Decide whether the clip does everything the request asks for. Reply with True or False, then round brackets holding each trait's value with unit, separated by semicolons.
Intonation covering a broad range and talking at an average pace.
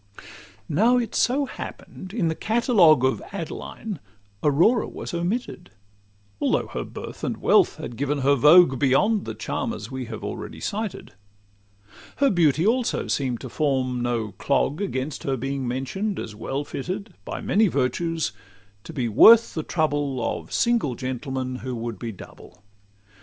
True (7.5 semitones; 150 wpm)